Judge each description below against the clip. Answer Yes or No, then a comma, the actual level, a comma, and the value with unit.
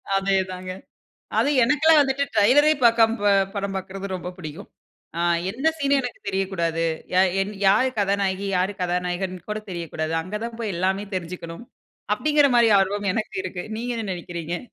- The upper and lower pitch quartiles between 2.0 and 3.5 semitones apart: No, average, 4.2 semitones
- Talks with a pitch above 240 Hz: No, high, 195 Hz